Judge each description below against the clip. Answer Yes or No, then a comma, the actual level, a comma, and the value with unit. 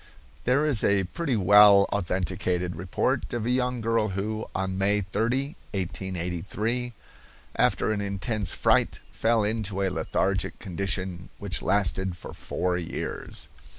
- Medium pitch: No, low, 100 Hz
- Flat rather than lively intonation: No, average, 3.2 semitones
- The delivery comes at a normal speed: No, slow, 130 wpm